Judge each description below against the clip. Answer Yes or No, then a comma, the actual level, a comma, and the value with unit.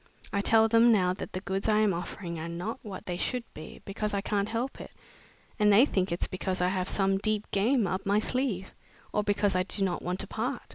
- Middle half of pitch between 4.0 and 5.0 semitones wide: No, average, 2.7 semitones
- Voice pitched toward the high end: Yes, high, 200 Hz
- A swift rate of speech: Yes, fast, 235 wpm